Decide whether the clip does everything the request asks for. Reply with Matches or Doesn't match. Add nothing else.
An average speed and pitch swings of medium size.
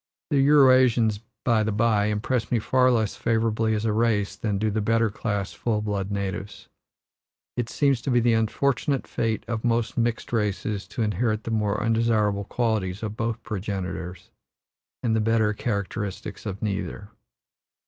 Doesn't match